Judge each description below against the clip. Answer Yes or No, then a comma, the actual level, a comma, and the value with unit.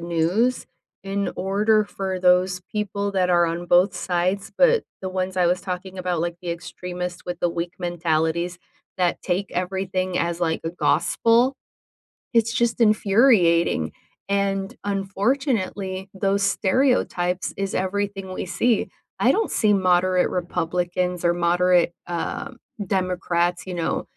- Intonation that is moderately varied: No, narrow, 2.2 semitones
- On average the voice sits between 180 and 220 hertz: Yes, medium, 185 Hz